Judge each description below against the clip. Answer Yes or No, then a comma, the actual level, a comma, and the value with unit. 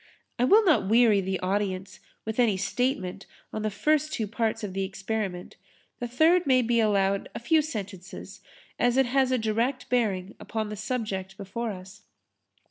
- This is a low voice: No, high, 220 Hz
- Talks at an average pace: Yes, average, 170 wpm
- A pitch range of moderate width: Yes, average, 4.3 semitones